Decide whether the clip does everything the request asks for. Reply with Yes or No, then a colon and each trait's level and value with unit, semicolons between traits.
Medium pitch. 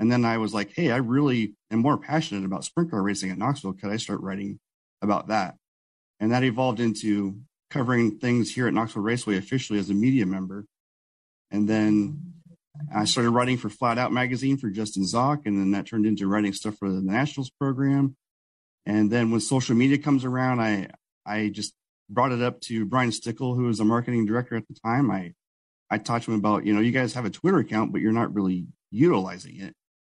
No: low, 115 Hz